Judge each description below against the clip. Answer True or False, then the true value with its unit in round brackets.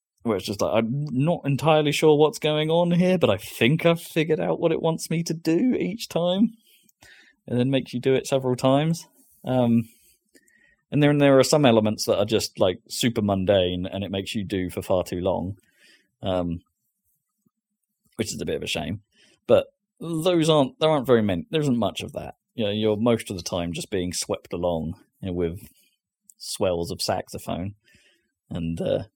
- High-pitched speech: False (135 Hz)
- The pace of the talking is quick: False (195 wpm)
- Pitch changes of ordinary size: False (8.4 semitones)